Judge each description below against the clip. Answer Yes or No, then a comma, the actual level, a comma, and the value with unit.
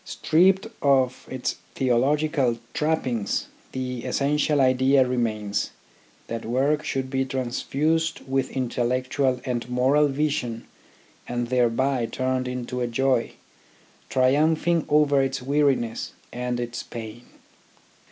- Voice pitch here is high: No, low, 130 Hz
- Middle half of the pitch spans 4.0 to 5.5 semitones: No, average, 2.7 semitones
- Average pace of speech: No, slow, 110 wpm